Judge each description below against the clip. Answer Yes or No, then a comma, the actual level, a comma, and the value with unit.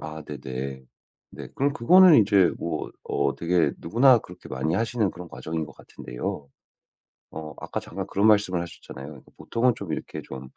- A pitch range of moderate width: No, wide, 6.3 semitones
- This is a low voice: Yes, very low, 85 Hz